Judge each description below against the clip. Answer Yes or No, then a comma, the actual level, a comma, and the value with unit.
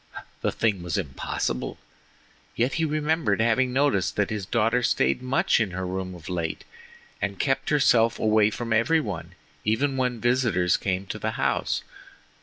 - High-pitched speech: No, low, 110 Hz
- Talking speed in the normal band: Yes, average, 160 wpm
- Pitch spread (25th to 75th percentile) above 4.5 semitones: Yes, average, 5.2 semitones